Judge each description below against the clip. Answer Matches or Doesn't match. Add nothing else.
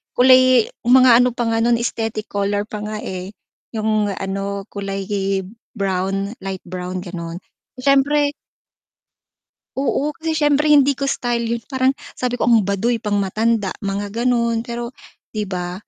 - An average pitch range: Matches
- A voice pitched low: Doesn't match